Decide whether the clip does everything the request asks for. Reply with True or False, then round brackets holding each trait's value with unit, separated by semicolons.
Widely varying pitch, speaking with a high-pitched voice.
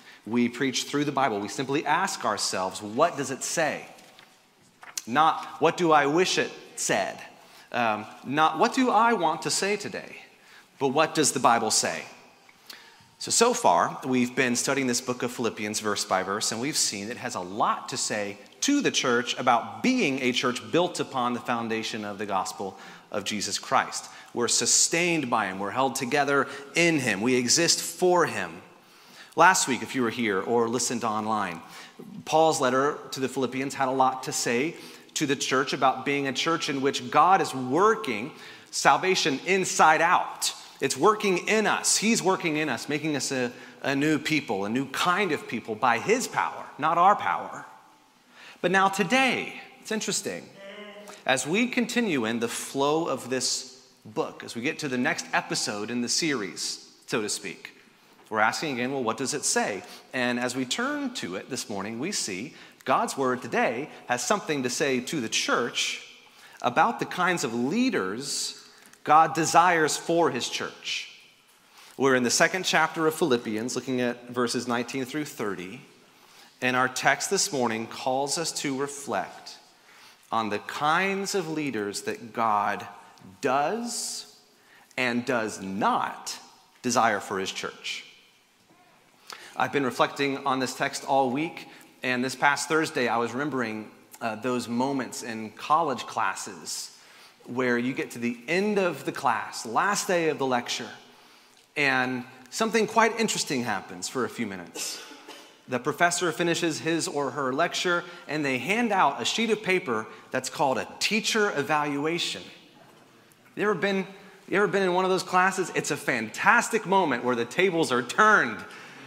False (6.1 semitones; 140 Hz)